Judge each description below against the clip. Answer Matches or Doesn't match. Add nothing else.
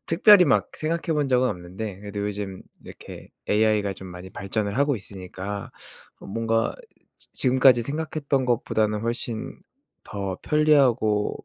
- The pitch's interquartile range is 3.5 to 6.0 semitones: Matches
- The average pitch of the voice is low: Matches